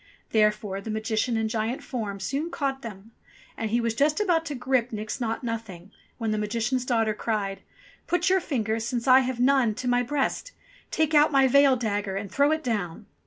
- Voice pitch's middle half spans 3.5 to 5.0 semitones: Yes, average, 3.9 semitones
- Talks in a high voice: Yes, high, 235 Hz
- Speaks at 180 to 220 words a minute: Yes, average, 200 wpm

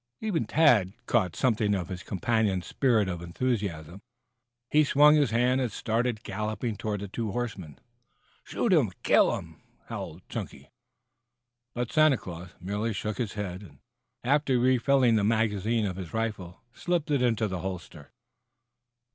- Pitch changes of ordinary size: Yes, average, 4.5 semitones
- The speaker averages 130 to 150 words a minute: Yes, average, 145 wpm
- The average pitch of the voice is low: Yes, low, 110 Hz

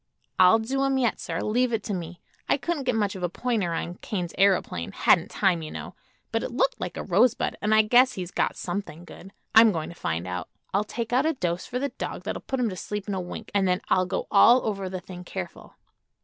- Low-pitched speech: No, high, 200 Hz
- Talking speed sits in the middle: No, fast, 245 wpm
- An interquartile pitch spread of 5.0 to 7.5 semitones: Yes, average, 5.3 semitones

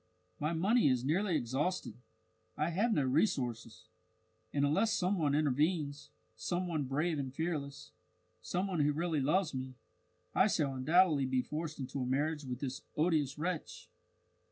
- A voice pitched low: No, medium, 150 Hz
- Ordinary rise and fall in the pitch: Yes, average, 4.3 semitones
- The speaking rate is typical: Yes, average, 155 wpm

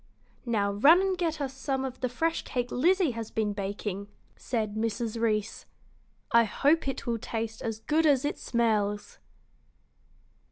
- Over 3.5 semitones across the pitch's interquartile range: Yes, average, 4.6 semitones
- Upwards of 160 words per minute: No, average, 155 wpm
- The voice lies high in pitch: Yes, high, 235 Hz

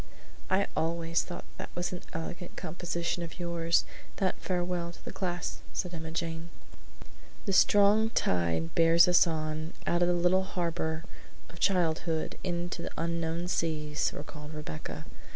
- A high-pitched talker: No, medium, 170 Hz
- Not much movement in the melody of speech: Yes, narrow, 1.6 semitones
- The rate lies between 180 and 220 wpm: No, average, 145 wpm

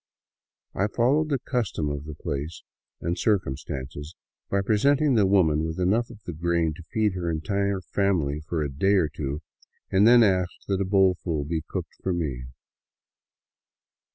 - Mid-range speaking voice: No, very low, 90 Hz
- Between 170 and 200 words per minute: No, average, 160 wpm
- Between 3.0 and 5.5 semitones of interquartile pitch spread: Yes, average, 4.7 semitones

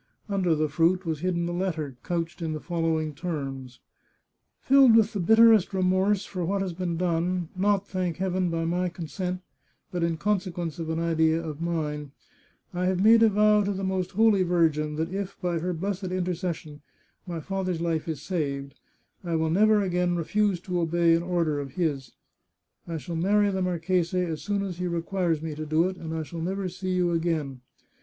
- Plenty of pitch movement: No, narrow, 2.6 semitones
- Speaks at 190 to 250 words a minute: Yes, average, 200 wpm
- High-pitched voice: No, medium, 175 Hz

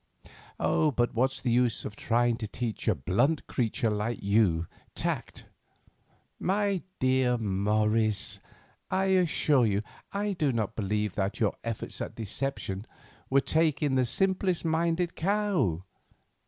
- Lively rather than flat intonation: Yes, wide, 7.0 semitones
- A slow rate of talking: Yes, slow, 130 wpm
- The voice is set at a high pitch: No, low, 120 Hz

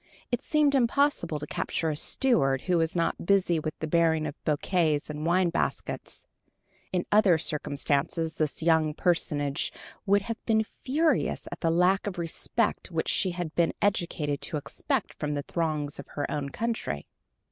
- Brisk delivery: No, average, 165 wpm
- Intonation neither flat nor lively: Yes, average, 4.3 semitones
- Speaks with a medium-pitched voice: Yes, medium, 165 Hz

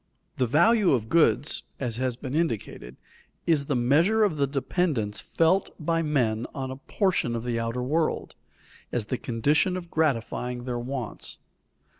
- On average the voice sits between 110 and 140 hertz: Yes, low, 135 Hz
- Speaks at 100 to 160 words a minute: Yes, average, 155 wpm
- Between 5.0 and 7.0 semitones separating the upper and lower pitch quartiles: Yes, average, 5.3 semitones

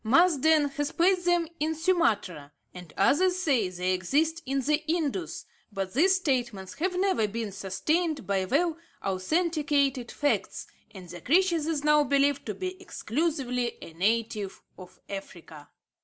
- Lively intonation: Yes, wide, 8.8 semitones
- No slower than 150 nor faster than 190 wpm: No, average, 140 wpm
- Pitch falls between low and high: No, very high, 280 Hz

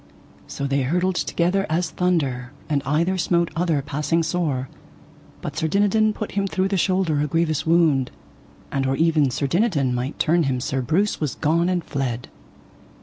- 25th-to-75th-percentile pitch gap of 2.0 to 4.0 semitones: No, average, 4.4 semitones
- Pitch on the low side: No, medium, 160 Hz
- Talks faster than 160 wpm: Yes, average, 170 wpm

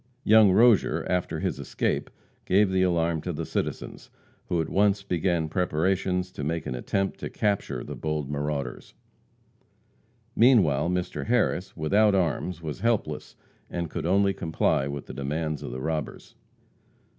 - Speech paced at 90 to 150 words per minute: Yes, average, 145 wpm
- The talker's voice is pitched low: Yes, very low, 85 Hz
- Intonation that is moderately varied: Yes, average, 4.1 semitones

